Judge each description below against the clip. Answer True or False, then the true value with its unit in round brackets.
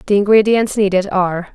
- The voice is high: True (200 Hz)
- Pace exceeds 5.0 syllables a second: True (6.0 syllables/s)